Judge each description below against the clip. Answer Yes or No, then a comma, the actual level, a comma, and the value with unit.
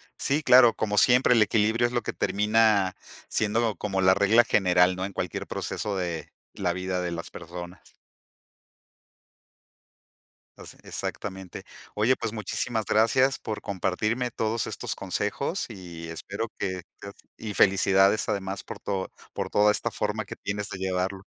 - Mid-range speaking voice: No, low, 100 Hz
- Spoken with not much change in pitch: No, average, 3.0 semitones